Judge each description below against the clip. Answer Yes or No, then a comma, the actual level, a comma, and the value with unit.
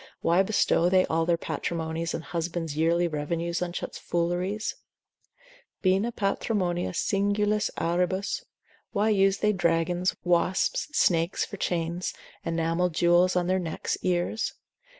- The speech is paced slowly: Yes, slow, 125 wpm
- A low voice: No, medium, 175 Hz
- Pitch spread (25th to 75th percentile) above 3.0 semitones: No, narrow, 2.4 semitones